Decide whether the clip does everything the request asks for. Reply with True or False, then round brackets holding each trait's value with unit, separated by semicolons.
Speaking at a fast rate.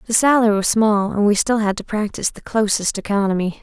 True (215 wpm)